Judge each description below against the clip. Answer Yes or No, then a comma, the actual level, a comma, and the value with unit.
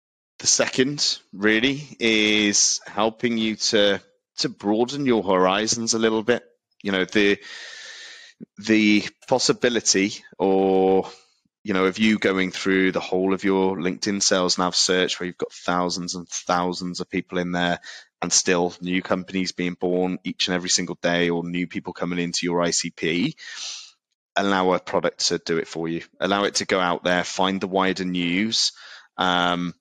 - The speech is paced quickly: No, average, 165 wpm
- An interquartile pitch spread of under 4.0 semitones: Yes, average, 3.1 semitones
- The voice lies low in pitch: Yes, very low, 95 Hz